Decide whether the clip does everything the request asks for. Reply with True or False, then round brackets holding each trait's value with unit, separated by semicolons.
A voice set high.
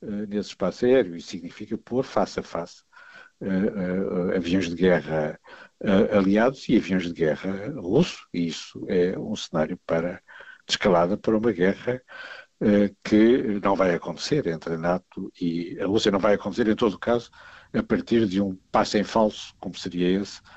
False (100 Hz)